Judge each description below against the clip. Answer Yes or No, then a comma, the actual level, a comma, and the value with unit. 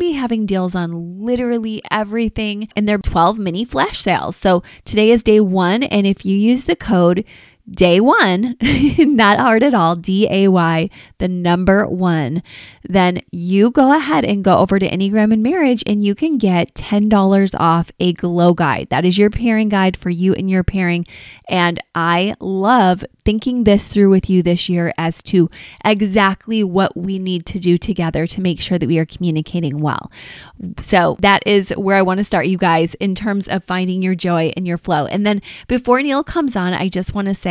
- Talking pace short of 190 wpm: No, average, 195 wpm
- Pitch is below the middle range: No, high, 195 Hz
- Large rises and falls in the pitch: No, average, 3.3 semitones